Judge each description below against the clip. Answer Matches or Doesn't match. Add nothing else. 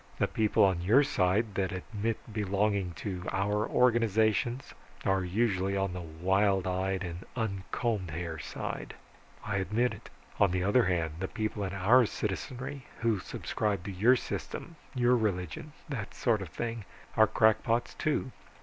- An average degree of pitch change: Matches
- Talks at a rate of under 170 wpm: Matches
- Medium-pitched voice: Doesn't match